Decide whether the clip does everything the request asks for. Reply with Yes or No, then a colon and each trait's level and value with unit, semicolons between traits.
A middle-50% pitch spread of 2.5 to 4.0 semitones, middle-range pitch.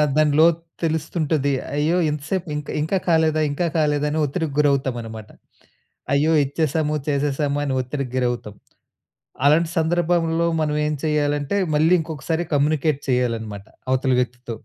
Yes: average, 2.8 semitones; medium, 150 Hz